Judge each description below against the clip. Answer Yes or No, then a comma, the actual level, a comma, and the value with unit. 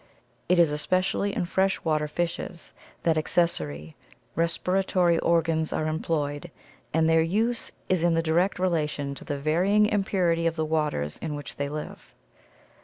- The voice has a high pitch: No, medium, 165 Hz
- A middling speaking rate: Yes, average, 145 wpm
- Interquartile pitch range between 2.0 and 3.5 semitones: Yes, average, 2.9 semitones